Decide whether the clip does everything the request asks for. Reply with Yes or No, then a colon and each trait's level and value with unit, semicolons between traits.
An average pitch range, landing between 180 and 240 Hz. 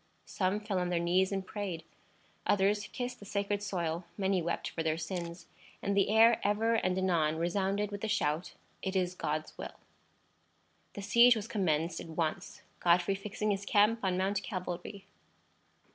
Yes: average, 3.0 semitones; high, 190 Hz